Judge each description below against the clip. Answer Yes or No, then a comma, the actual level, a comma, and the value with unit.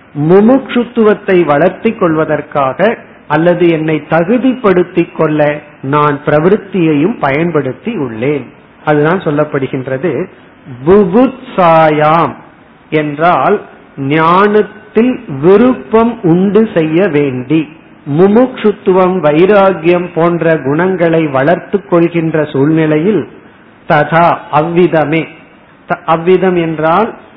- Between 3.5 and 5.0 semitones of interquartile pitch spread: Yes, average, 4.5 semitones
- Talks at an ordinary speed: No, slow, 65 wpm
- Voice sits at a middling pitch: Yes, medium, 170 Hz